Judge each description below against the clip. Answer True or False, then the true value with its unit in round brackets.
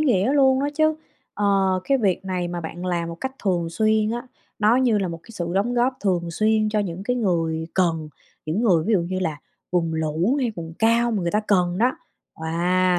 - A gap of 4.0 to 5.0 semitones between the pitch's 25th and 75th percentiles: True (4.7 semitones)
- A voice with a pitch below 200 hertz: True (190 Hz)